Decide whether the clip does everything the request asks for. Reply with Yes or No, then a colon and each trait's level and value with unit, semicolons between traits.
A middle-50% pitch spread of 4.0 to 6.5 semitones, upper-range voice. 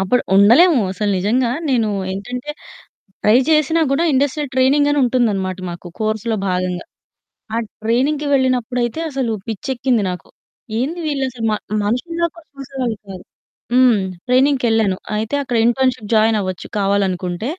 Yes: average, 4.3 semitones; high, 240 Hz